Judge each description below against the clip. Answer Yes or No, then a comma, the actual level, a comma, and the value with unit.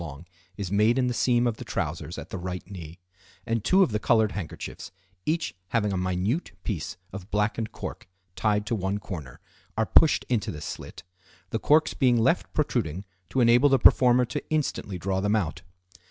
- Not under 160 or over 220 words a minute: Yes, average, 185 wpm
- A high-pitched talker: No, low, 105 Hz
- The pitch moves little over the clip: No, average, 4.4 semitones